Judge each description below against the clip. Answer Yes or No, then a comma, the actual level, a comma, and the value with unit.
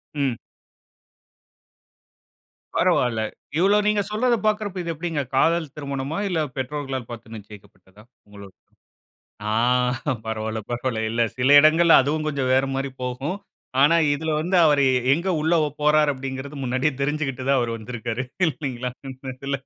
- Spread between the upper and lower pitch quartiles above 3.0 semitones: Yes, average, 4.1 semitones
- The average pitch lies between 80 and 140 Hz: Yes, low, 135 Hz